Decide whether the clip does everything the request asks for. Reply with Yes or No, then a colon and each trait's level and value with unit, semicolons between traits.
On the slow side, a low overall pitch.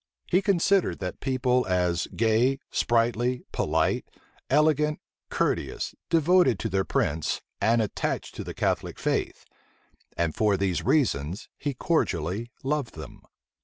Yes: slow, 125 wpm; low, 120 Hz